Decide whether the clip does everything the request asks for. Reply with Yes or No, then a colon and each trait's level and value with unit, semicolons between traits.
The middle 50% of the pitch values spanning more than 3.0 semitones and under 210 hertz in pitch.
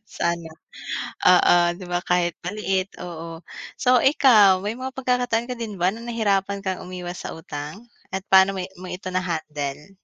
Yes: average, 3.4 semitones; high, 190 Hz